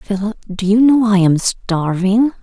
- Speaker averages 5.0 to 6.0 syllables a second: No, 4.1 syllables/s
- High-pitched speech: Yes, high, 205 Hz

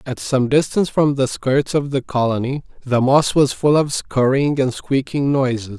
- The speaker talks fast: No, average, 185 wpm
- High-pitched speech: No, low, 135 Hz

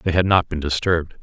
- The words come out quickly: Yes, fast, 245 wpm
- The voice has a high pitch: No, very low, 85 Hz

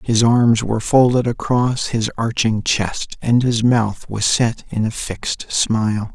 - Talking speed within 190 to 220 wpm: No, average, 165 wpm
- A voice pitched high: No, low, 115 Hz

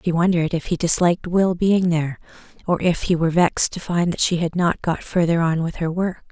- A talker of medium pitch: Yes, medium, 170 Hz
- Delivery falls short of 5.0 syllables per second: No, 5.8 syllables/s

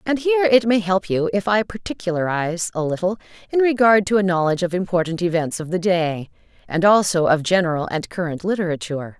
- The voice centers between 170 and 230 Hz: Yes, medium, 185 Hz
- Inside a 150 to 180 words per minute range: No, average, 190 wpm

